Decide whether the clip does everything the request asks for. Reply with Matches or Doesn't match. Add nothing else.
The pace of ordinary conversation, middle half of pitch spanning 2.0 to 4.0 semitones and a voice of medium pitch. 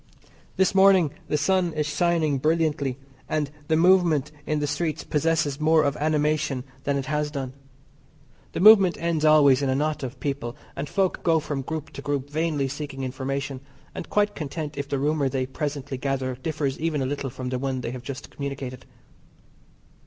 Matches